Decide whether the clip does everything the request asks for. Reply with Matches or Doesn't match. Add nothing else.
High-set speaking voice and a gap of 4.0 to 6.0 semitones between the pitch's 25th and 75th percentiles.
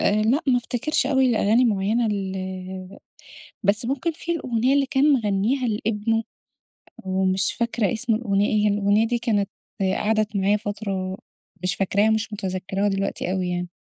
Doesn't match